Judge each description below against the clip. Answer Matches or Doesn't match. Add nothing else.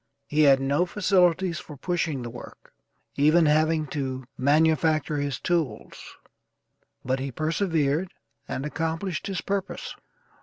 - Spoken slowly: Matches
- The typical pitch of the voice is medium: Matches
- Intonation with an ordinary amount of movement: Matches